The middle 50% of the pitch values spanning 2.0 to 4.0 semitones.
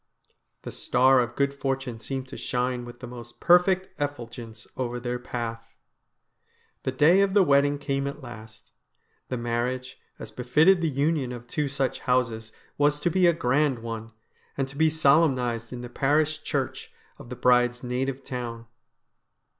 Yes: average, 3.0 semitones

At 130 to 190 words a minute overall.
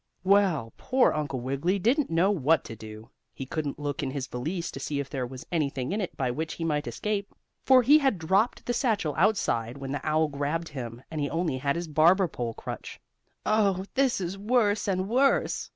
No: fast, 205 wpm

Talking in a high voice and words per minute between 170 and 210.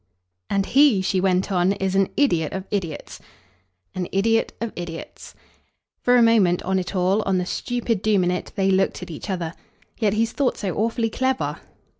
Yes: high, 195 Hz; average, 185 wpm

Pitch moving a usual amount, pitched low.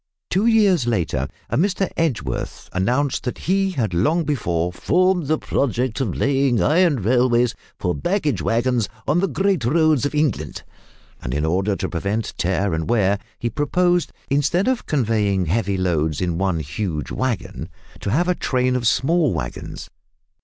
No: wide, 8.7 semitones; low, 125 Hz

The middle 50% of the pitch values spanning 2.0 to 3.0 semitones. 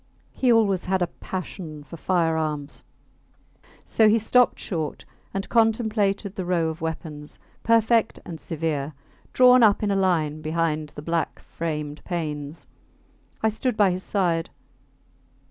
No: average, 5.1 semitones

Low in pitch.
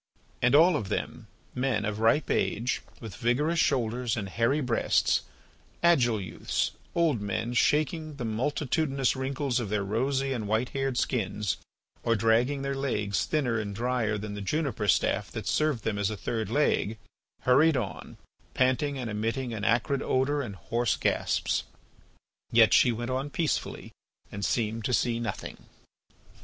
Yes: low, 120 Hz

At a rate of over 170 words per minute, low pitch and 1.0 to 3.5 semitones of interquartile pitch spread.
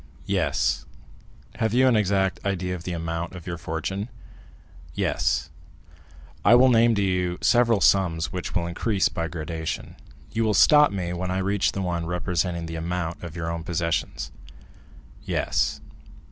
No: average, 155 wpm; very low, 90 Hz; average, 3.1 semitones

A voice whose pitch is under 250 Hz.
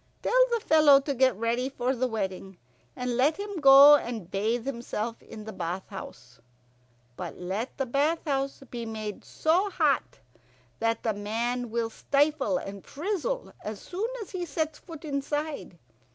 No: very high, 260 Hz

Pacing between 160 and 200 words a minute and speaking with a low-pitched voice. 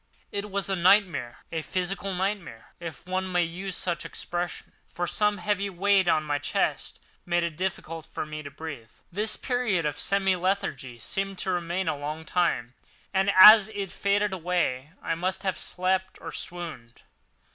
No: average, 170 wpm; medium, 180 Hz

